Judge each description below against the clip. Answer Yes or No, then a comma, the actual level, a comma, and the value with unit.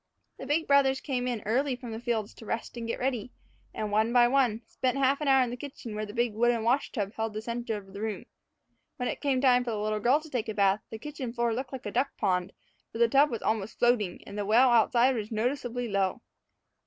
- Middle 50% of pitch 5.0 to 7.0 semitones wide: No, average, 3.1 semitones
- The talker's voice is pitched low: No, high, 235 Hz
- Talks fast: Yes, fast, 250 wpm